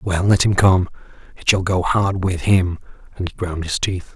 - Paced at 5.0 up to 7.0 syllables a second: No, 4.6 syllables/s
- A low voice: Yes, very low, 90 Hz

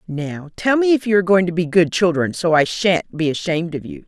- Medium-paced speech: No, fast, 265 wpm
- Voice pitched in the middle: Yes, medium, 175 Hz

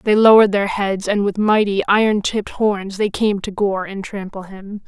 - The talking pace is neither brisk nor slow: No, fast, 210 wpm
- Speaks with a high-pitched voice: Yes, high, 200 Hz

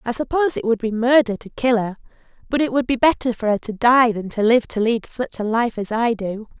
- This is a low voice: No, high, 235 Hz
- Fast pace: Yes, fast, 265 wpm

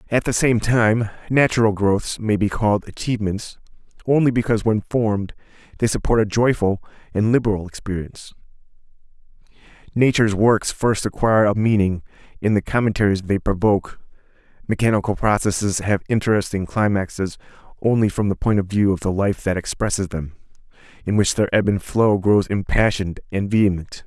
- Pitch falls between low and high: No, low, 105 Hz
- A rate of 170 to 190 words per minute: No, average, 145 wpm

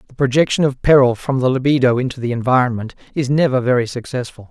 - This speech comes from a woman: No, male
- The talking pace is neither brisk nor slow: Yes, average, 185 wpm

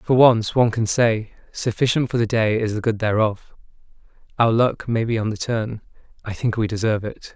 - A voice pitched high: No, low, 115 Hz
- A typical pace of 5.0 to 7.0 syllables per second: Yes, 5.3 syllables/s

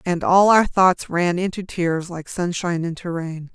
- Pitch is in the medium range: Yes, medium, 175 Hz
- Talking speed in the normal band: Yes, average, 185 wpm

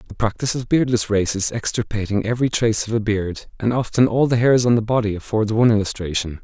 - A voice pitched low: Yes, low, 110 Hz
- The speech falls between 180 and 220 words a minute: Yes, fast, 205 wpm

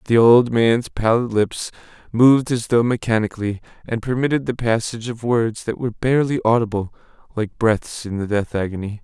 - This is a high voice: No, low, 115 Hz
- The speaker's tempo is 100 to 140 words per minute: No, average, 165 wpm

